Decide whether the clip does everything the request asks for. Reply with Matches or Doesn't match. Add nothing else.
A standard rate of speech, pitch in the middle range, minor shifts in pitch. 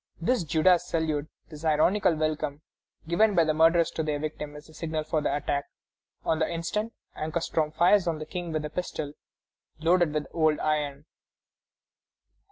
Matches